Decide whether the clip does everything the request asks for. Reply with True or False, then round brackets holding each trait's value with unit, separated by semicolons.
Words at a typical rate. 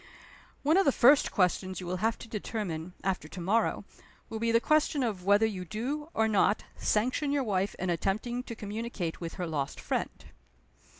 True (185 wpm)